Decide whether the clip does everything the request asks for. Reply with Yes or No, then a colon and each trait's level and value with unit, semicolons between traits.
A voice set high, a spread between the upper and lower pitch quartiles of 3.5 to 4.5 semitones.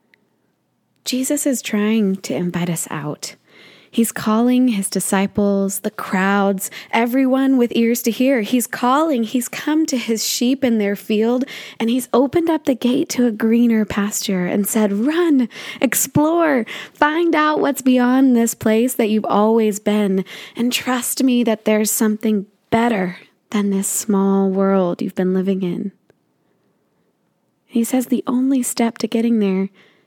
Yes: high, 230 Hz; average, 4.0 semitones